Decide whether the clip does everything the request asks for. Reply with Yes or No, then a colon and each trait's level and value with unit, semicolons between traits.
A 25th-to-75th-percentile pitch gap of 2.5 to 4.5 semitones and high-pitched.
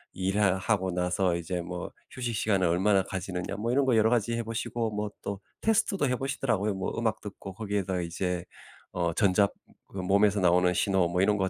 No: average, 3.3 semitones; low, 100 Hz